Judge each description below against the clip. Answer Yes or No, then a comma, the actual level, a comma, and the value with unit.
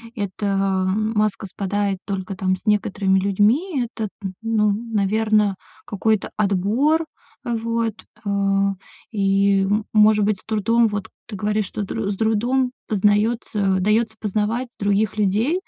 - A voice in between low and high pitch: No, high, 210 Hz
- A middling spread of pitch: No, narrow, 1.9 semitones